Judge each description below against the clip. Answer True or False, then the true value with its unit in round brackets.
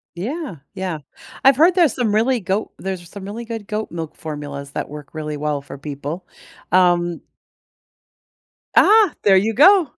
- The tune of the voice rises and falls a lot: True (7.2 semitones)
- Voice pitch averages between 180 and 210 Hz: True (190 Hz)